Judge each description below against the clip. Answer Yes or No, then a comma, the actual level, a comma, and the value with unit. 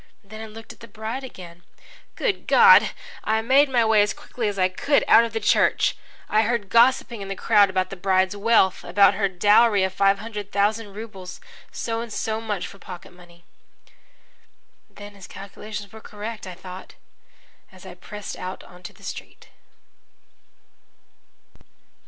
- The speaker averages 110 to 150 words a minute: No, average, 165 wpm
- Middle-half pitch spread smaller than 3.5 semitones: Yes, average, 2.9 semitones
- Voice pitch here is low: No, high, 205 Hz